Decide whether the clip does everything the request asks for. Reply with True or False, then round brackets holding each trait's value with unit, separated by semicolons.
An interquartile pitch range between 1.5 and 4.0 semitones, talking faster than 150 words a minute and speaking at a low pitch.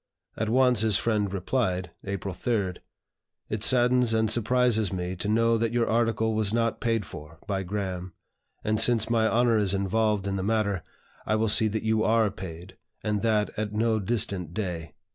True (2.7 semitones; 180 wpm; 110 Hz)